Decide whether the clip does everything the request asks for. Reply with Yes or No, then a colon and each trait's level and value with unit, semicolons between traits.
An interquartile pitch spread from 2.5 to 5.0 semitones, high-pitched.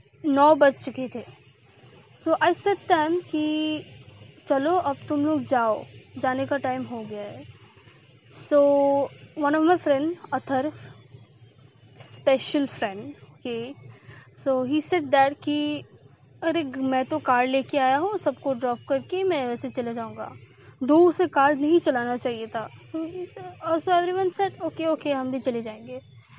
No: wide, 5.4 semitones; very high, 275 Hz